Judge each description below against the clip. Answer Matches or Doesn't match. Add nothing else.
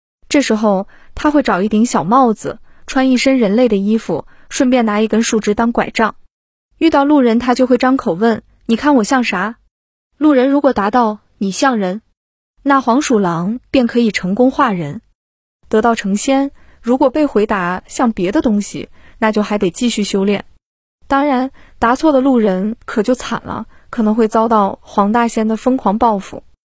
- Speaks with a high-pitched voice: Matches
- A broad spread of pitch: Doesn't match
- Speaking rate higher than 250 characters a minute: Doesn't match